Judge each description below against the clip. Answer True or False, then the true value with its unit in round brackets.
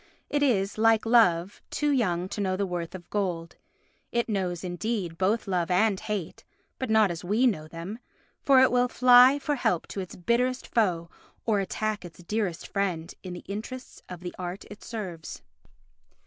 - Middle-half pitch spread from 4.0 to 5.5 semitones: True (4.6 semitones)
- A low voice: False (200 Hz)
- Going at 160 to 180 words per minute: True (175 wpm)